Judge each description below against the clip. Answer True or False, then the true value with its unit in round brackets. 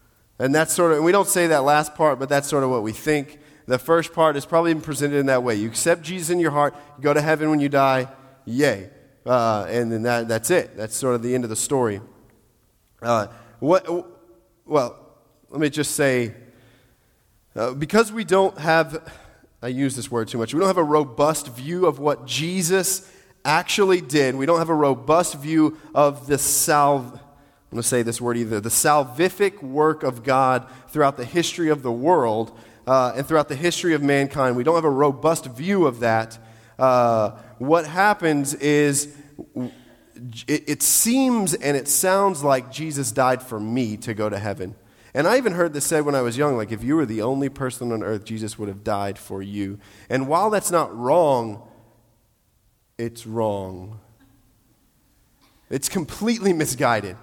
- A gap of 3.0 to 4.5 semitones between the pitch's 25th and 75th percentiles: False (5.0 semitones)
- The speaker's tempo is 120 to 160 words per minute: False (185 wpm)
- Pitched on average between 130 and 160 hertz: True (140 Hz)